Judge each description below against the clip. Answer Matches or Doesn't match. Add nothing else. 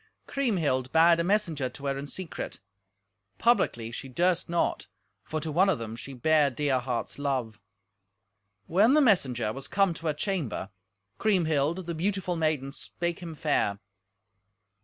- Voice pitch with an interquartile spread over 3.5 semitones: Matches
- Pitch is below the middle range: Doesn't match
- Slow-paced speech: Doesn't match